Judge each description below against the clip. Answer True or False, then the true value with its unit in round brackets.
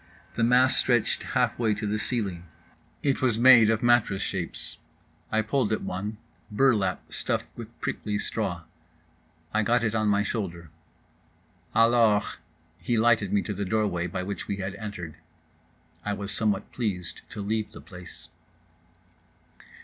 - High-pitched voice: False (105 Hz)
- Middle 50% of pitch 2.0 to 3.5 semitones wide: True (2.7 semitones)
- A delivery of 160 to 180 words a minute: False (145 wpm)